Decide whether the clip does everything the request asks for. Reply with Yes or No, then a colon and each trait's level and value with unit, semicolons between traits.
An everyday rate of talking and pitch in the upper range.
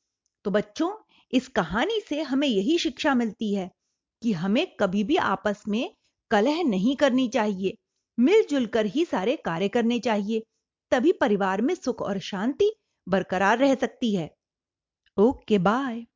Yes: average, 145 wpm; high, 235 Hz